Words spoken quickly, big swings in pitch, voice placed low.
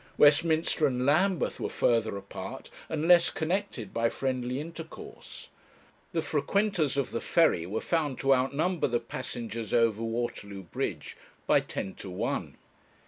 No: average, 140 wpm; wide, 5.8 semitones; low, 130 Hz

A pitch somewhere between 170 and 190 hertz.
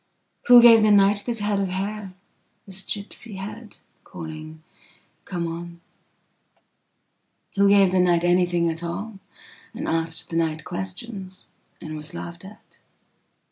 Yes: medium, 185 Hz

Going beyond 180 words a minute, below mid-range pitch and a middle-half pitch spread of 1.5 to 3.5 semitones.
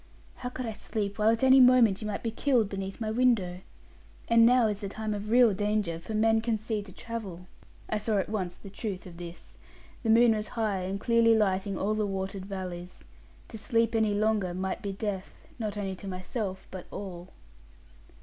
No: average, 200 wpm; high, 210 Hz; average, 2.9 semitones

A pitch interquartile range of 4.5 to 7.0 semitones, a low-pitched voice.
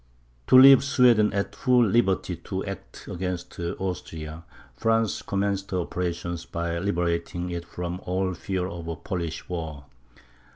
No: average, 2.9 semitones; very low, 90 Hz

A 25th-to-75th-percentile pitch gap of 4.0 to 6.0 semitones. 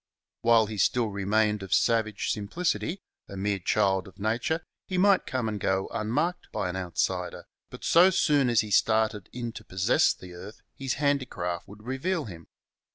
Yes: wide, 5.4 semitones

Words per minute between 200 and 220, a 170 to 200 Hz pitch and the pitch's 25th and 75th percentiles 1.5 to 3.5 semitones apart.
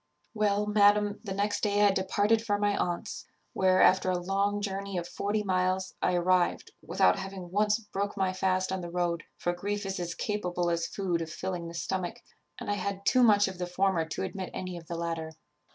Yes: fast, 205 wpm; high, 190 Hz; narrow, 2.5 semitones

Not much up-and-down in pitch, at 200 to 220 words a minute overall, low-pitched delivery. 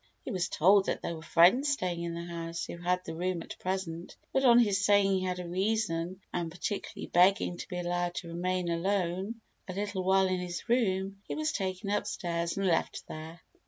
No: narrow, 2.3 semitones; fast, 205 wpm; medium, 185 Hz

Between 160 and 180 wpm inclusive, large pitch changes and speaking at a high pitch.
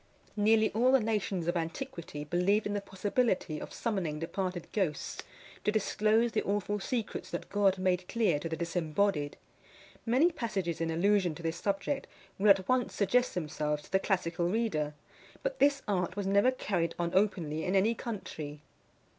No: average, 165 wpm; average, 4.3 semitones; high, 195 Hz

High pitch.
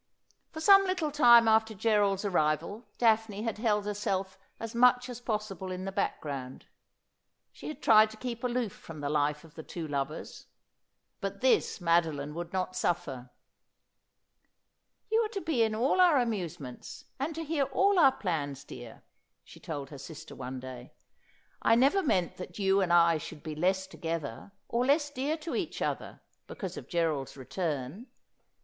Yes: high, 195 Hz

